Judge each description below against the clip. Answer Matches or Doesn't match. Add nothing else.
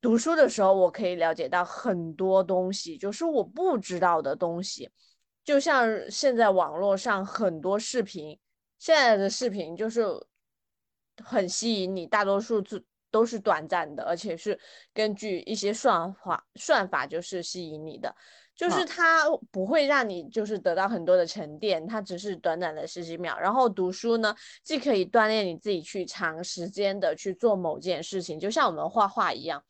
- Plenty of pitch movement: Doesn't match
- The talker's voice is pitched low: Doesn't match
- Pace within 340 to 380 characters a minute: Doesn't match